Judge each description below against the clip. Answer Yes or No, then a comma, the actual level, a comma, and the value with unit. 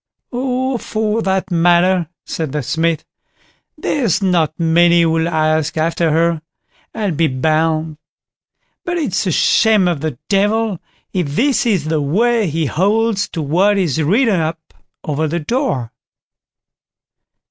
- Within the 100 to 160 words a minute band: Yes, slow, 135 wpm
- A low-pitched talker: No, medium, 170 Hz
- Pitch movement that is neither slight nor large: Yes, average, 4.9 semitones